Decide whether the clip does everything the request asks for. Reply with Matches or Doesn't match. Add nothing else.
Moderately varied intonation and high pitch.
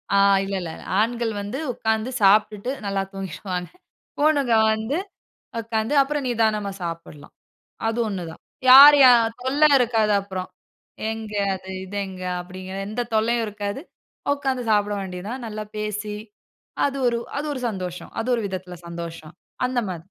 Matches